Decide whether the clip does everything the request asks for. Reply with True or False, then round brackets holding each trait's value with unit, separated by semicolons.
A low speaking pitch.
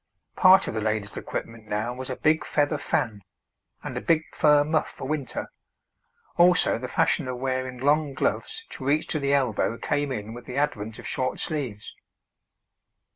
True (130 Hz)